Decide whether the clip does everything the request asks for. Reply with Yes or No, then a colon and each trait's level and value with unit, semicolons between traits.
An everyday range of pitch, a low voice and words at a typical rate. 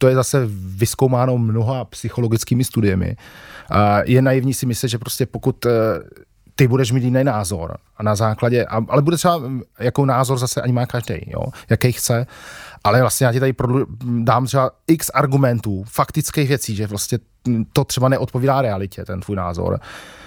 Yes: average, 3.1 semitones; low, 125 Hz; average, 155 wpm